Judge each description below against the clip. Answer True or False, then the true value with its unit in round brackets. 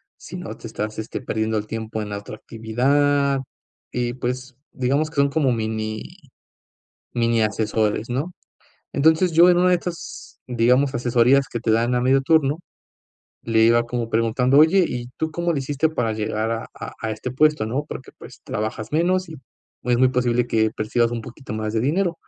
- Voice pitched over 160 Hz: False (125 Hz)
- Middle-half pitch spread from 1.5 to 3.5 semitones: False (4.2 semitones)